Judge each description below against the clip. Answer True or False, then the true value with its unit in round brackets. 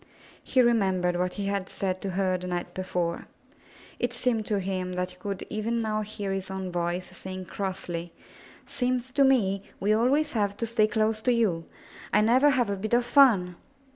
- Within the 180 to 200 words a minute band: True (195 wpm)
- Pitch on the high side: True (200 Hz)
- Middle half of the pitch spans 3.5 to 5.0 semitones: True (4.1 semitones)